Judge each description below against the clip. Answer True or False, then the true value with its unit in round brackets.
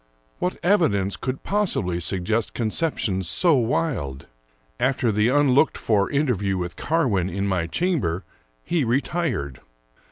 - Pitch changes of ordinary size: False (8.2 semitones)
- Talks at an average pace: False (120 wpm)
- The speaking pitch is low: True (115 Hz)